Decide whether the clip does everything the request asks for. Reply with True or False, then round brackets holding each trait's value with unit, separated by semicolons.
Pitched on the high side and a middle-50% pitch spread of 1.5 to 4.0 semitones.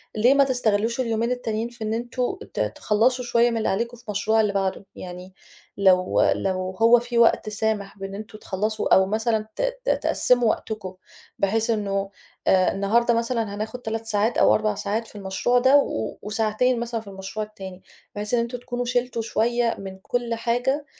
True (220 Hz; 3.0 semitones)